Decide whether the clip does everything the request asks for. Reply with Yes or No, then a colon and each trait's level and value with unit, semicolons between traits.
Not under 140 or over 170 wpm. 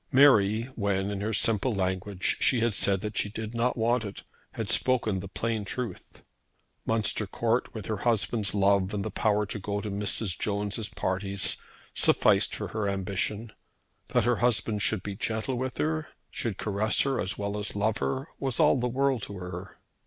No: average, 180 wpm